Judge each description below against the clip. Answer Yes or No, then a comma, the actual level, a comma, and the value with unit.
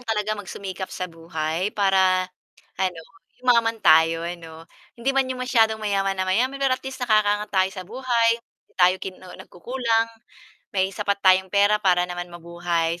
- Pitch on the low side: No, high, 195 Hz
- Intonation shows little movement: No, average, 4.2 semitones